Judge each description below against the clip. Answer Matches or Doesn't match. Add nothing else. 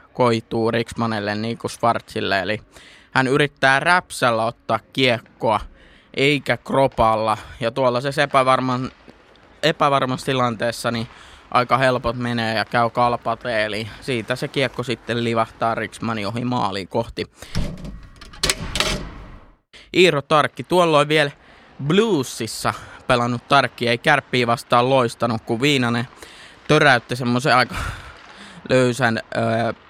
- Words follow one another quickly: Doesn't match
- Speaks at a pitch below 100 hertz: Doesn't match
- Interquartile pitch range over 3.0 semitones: Doesn't match